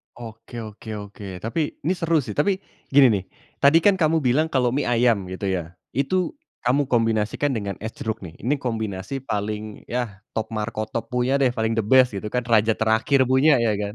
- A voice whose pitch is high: No, low, 115 Hz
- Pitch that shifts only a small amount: No, average, 4.0 semitones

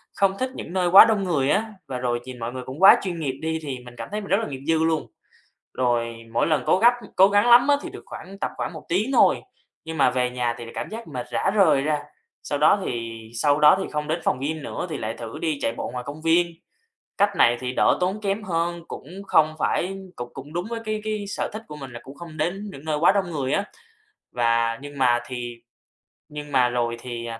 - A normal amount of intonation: No, wide, 7.1 semitones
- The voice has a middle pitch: Yes, medium, 150 Hz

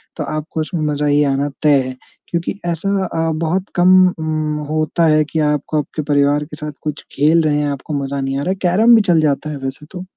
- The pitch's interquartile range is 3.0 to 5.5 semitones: No, narrow, 2.5 semitones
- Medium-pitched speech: Yes, medium, 155 Hz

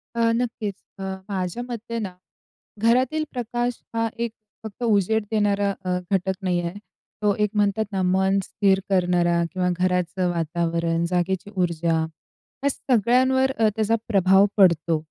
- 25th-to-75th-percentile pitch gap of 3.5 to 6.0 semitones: Yes, average, 4.1 semitones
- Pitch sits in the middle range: No, high, 195 Hz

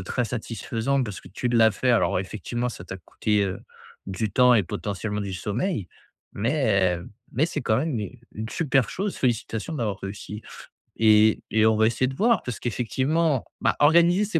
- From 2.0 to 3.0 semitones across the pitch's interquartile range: No, average, 4.2 semitones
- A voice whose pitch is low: Yes, low, 115 Hz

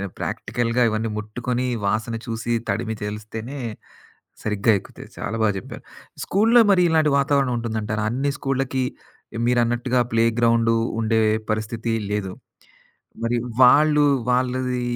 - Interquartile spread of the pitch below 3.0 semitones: Yes, narrow, 2.6 semitones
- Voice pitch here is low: Yes, low, 115 Hz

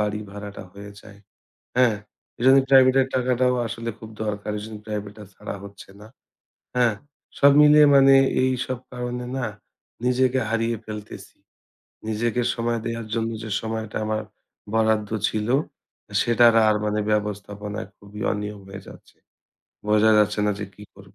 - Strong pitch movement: No, average, 2.8 semitones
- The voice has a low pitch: Yes, low, 110 Hz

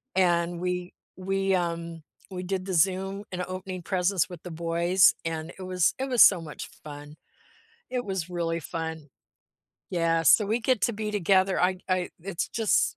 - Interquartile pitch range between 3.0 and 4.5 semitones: No, narrow, 2.4 semitones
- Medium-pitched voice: Yes, medium, 180 Hz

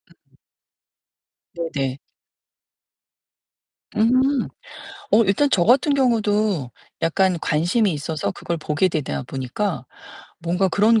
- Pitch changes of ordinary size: No, wide, 6.2 semitones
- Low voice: No, medium, 185 Hz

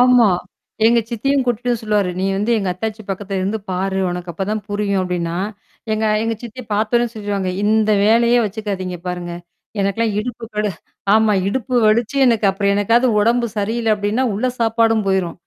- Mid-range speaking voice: No, high, 210 Hz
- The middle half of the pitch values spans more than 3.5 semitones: No, average, 2.8 semitones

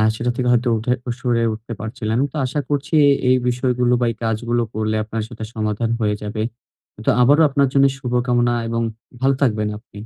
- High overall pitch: No, low, 120 Hz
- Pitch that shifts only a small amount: Yes, narrow, 2.3 semitones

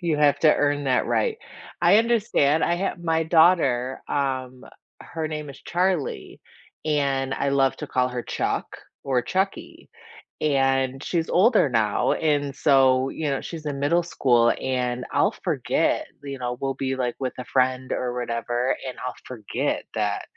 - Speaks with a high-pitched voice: No, low, 135 Hz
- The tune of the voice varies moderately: Yes, average, 3.8 semitones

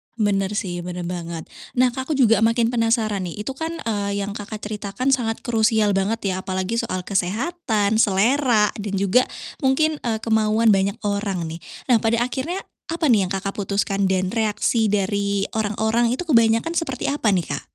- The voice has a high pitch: Yes, high, 215 Hz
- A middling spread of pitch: Yes, average, 3.3 semitones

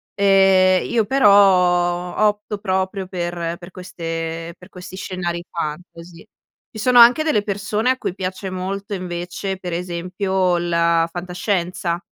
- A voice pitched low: No, medium, 185 Hz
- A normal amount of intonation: No, narrow, 2.3 semitones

